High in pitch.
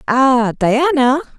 Yes: high, 240 Hz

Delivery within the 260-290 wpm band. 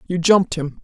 No: fast, 215 wpm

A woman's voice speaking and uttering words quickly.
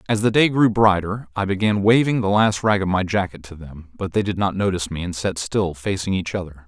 No: male; fast, 250 wpm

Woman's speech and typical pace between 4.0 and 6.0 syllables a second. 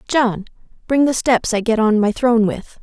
Yes: female; 4.9 syllables/s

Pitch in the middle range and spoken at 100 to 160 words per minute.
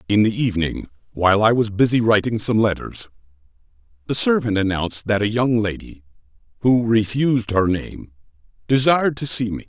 No: low, 105 Hz; average, 155 wpm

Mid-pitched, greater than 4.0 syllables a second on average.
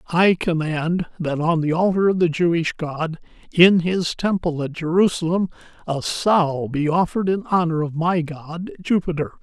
Yes: medium, 170 Hz; 4.5 syllables/s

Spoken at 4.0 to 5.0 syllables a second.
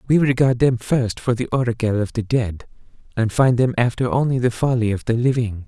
No: 5.5 syllables/s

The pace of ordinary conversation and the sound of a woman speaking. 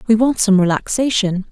Yes: average, 160 wpm; female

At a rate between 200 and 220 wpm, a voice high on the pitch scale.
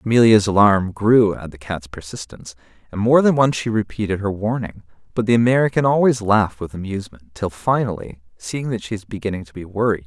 No: fast, 205 wpm; low, 105 Hz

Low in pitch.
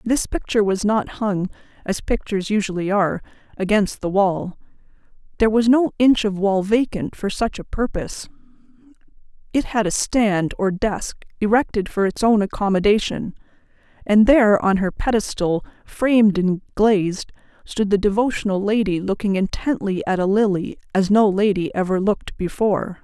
No: high, 205 Hz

